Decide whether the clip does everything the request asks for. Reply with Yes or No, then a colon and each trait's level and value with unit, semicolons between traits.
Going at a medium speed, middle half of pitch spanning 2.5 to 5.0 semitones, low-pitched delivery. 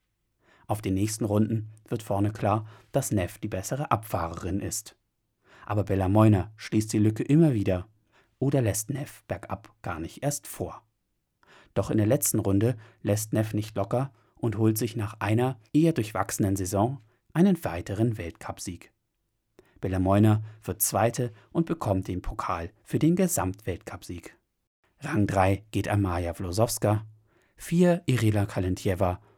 Yes: average, 135 wpm; average, 3.0 semitones; low, 105 Hz